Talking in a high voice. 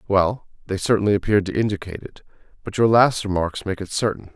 No: low, 100 Hz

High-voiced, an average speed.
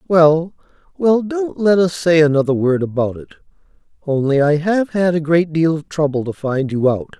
No: medium, 160 Hz; average, 190 wpm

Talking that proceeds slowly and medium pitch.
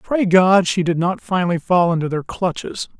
No: average, 200 wpm; medium, 180 Hz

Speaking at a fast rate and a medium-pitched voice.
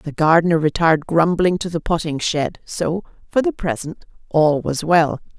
No: average, 165 wpm; medium, 165 Hz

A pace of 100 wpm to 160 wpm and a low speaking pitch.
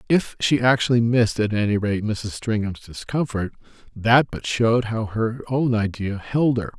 No: average, 170 wpm; low, 115 Hz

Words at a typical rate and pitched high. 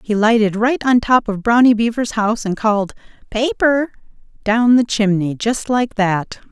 Yes: average, 155 wpm; high, 225 Hz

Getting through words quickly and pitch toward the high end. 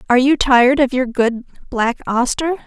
No: average, 180 wpm; very high, 255 Hz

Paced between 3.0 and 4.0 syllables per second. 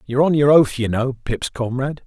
No: 6.0 syllables/s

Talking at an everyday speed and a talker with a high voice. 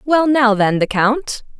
Yes: average, 190 wpm; high, 245 Hz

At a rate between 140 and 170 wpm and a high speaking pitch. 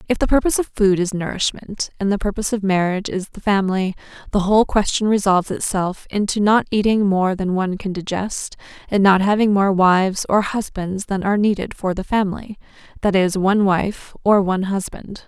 No: average, 185 wpm; high, 195 Hz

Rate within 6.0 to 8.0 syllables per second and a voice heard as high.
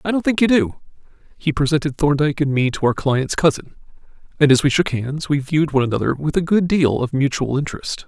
No: 6.3 syllables/s; medium, 145 Hz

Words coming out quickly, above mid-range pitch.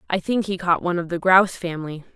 No: fast, 250 wpm; medium, 180 Hz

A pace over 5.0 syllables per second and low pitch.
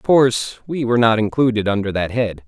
Yes: 6.0 syllables/s; low, 115 Hz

